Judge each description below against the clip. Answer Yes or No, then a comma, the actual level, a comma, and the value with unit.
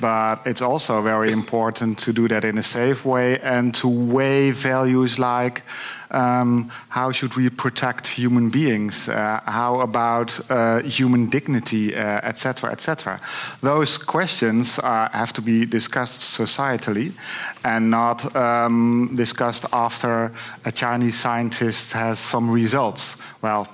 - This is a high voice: No, low, 120 Hz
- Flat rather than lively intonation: Yes, narrow, 1.8 semitones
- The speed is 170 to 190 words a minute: No, average, 140 wpm